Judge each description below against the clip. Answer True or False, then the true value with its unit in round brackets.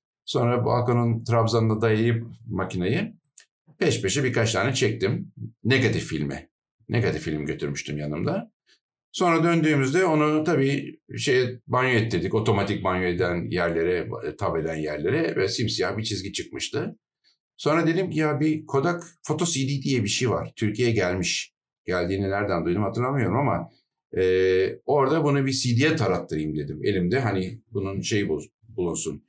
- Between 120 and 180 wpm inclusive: True (135 wpm)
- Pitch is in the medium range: False (115 Hz)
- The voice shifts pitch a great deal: True (6.8 semitones)